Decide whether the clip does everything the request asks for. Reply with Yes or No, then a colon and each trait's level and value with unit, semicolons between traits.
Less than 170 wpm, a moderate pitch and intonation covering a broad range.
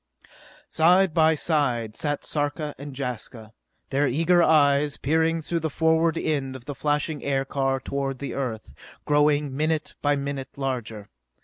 No: average, 140 wpm; medium, 145 Hz; average, 2.8 semitones